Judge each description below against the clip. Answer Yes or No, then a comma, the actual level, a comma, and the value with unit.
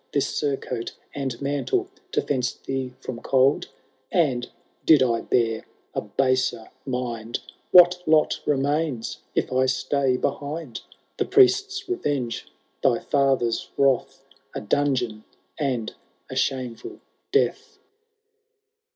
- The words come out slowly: Yes, slow, 110 wpm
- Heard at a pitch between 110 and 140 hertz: Yes, low, 135 Hz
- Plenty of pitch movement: No, average, 2.8 semitones